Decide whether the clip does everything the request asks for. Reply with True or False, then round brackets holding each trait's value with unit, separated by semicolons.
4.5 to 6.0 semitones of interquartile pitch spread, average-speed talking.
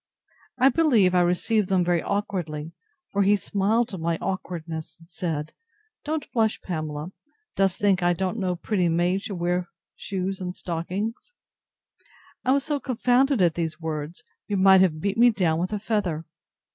False (3.6 semitones; 165 wpm)